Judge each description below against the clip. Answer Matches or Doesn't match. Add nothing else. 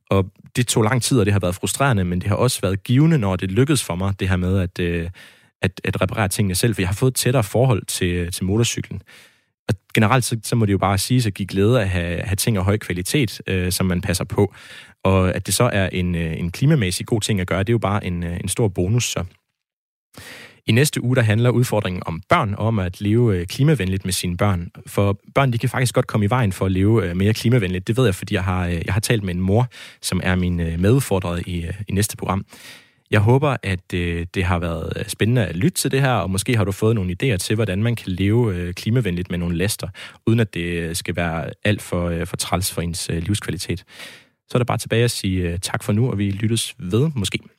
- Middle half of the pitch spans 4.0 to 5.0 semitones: Matches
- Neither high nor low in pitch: Doesn't match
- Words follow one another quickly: Matches